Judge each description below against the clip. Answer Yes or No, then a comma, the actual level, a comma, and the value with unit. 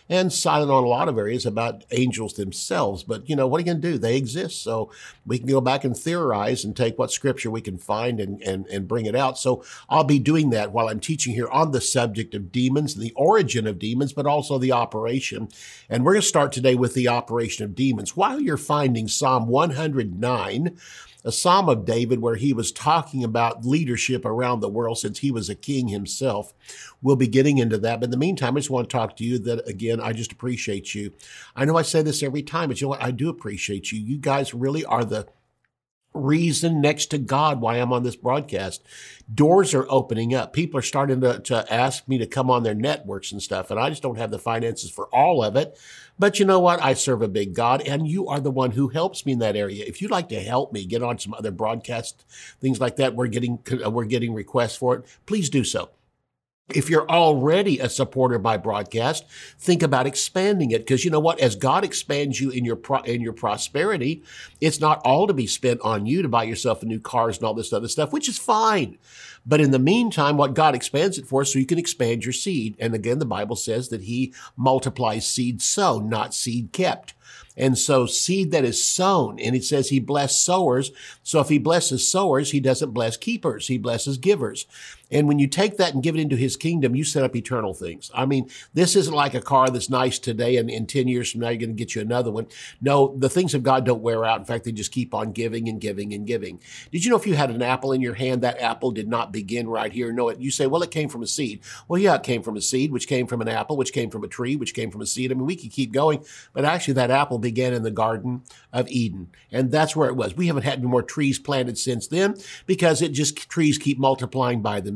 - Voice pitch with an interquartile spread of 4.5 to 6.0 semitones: No, average, 3.7 semitones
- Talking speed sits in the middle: No, fast, 245 wpm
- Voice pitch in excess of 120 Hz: Yes, low, 130 Hz